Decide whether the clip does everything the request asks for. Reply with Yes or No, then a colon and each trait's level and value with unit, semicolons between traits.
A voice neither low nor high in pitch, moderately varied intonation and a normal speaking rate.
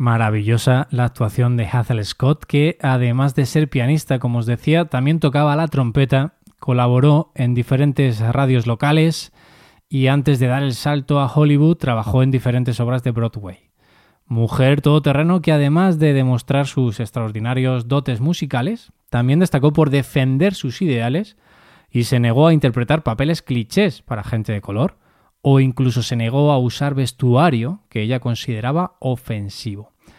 No: low, 130 Hz; average, 3.4 semitones; average, 150 wpm